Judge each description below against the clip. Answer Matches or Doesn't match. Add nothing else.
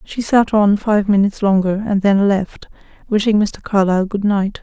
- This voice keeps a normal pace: Matches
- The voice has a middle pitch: Doesn't match